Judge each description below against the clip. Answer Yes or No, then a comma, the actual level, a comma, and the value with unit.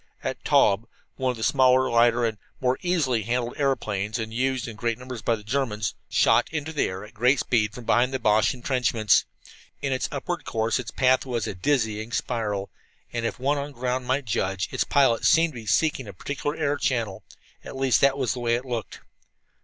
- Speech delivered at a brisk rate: Yes, fast, 210 wpm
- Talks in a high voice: No, low, 125 Hz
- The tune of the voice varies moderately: Yes, average, 3.2 semitones